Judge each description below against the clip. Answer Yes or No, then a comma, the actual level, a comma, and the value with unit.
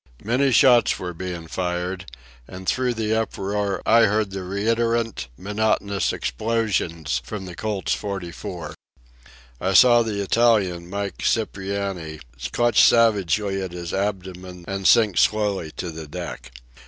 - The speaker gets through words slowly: Yes, slow, 130 wpm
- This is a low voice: Yes, low, 100 Hz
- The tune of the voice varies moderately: Yes, average, 3.5 semitones